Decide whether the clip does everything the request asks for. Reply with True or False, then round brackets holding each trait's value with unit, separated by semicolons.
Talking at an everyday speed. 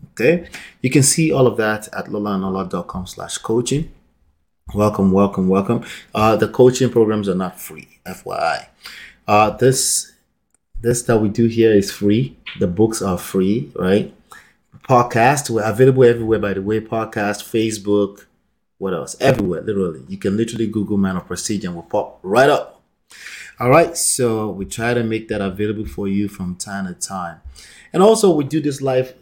True (170 wpm)